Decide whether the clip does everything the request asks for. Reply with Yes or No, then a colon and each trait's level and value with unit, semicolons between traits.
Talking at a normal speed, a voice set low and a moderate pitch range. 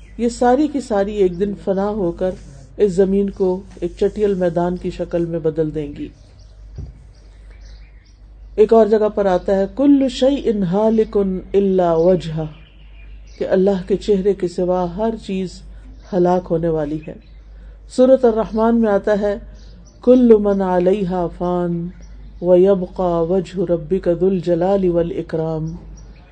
No: average, 135 wpm; medium, 185 Hz; average, 3.0 semitones